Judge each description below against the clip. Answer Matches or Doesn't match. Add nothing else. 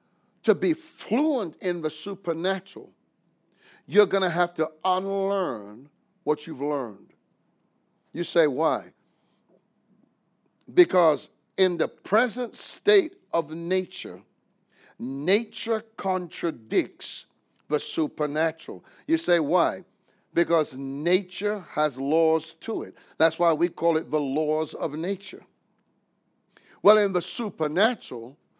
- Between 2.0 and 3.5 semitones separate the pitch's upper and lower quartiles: Doesn't match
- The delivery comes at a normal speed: Doesn't match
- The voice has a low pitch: Doesn't match